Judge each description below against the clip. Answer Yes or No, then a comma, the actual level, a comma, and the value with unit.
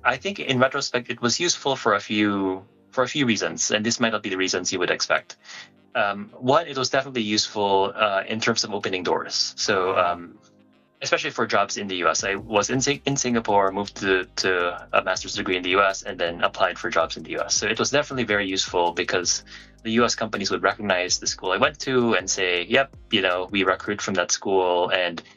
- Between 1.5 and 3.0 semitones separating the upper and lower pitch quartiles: No, average, 4.5 semitones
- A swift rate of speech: Yes, fast, 220 wpm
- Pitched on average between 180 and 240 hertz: No, low, 105 Hz